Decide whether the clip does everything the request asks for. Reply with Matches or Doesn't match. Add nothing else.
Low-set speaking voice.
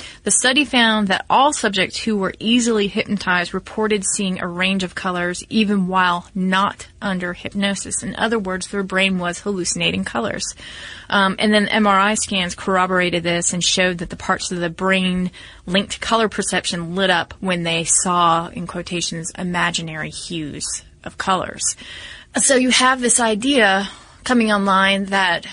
Doesn't match